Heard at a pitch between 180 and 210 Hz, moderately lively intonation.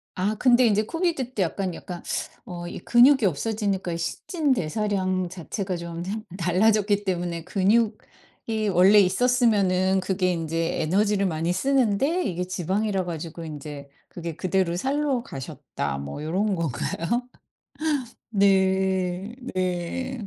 Yes: high, 190 Hz; average, 3.8 semitones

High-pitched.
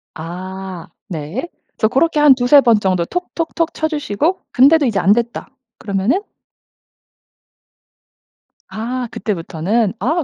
Yes: high, 235 Hz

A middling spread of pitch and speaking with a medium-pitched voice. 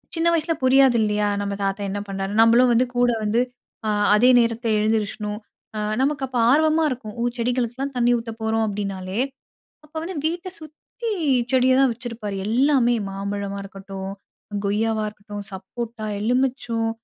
No: average, 3.9 semitones; high, 230 Hz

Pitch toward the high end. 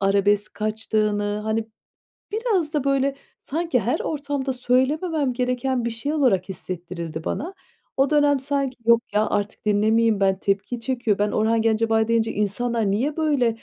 Yes: high, 230 Hz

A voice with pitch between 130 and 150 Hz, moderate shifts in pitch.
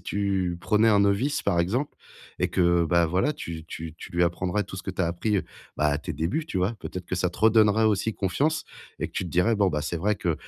No: very low, 95 Hz; average, 3.5 semitones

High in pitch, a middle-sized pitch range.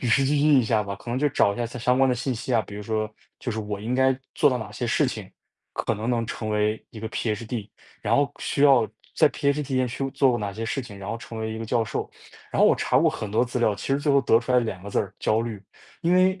No: low, 115 Hz; average, 3.4 semitones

